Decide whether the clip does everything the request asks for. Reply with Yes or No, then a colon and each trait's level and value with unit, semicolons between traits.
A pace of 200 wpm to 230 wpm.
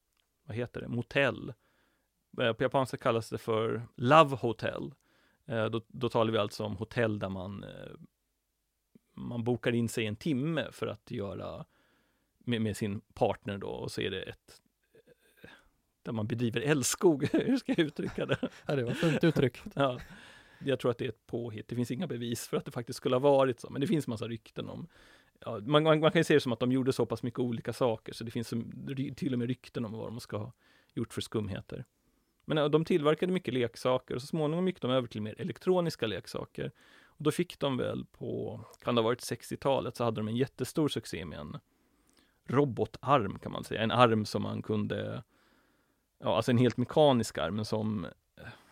Yes: fast, 205 wpm